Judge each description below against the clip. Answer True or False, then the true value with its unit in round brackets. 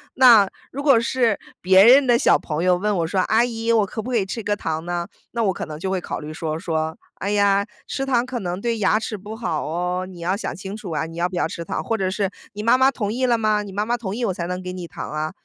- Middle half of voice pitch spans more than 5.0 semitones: False (4.4 semitones)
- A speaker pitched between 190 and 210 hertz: True (200 Hz)